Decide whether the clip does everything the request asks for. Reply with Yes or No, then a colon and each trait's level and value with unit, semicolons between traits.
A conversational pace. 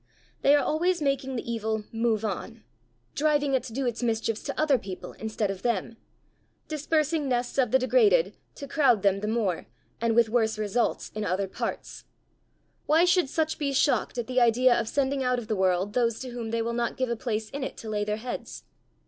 No: fast, 210 wpm